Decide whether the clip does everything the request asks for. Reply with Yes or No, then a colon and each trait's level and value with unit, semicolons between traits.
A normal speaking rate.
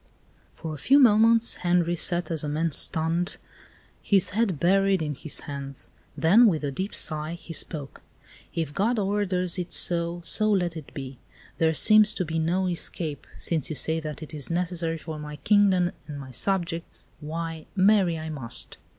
Yes: average, 175 wpm